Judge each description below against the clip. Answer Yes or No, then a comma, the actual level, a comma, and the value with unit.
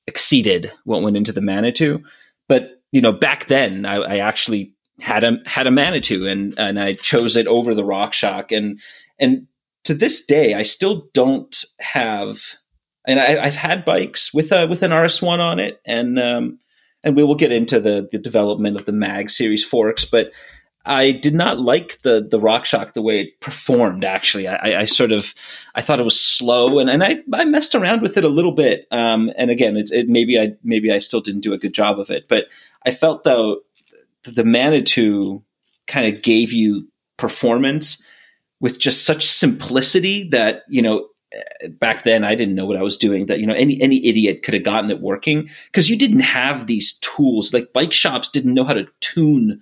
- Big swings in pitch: Yes, wide, 6.5 semitones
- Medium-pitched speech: No, low, 120 Hz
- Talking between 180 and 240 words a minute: Yes, average, 200 wpm